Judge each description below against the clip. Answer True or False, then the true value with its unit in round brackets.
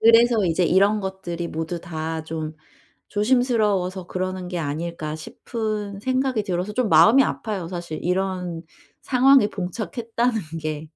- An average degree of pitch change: True (4.5 semitones)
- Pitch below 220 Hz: True (190 Hz)